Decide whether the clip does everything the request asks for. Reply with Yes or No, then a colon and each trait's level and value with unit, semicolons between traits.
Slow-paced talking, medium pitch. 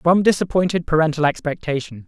Yes: slow, 115 wpm; medium, 160 Hz